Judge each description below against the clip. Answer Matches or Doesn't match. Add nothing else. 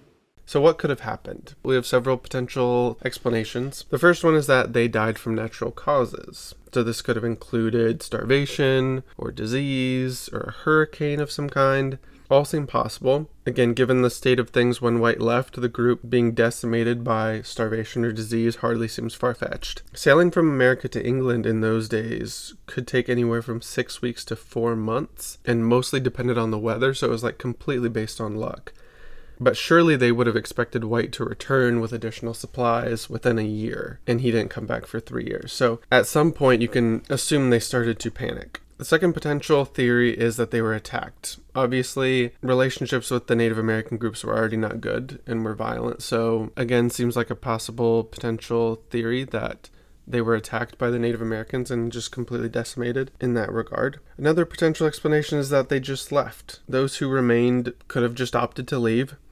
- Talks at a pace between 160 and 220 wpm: Matches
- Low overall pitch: Matches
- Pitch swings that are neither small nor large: Doesn't match